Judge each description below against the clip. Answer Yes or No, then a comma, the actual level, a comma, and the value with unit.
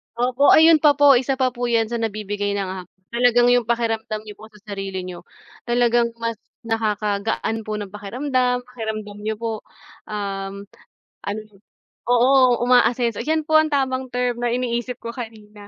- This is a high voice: Yes, high, 235 Hz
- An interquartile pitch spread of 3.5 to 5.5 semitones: No, average, 2.9 semitones